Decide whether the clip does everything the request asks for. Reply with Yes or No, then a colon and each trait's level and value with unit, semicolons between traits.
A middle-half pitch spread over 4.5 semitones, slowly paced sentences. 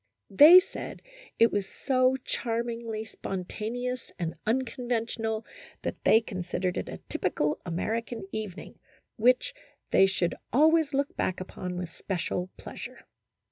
Yes: average, 4.9 semitones; slow, 125 wpm